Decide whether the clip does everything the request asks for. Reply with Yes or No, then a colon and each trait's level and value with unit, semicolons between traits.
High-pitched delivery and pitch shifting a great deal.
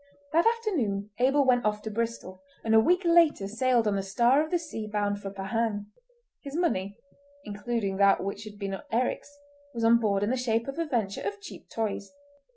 Yes: high, 230 Hz; wide, 5.8 semitones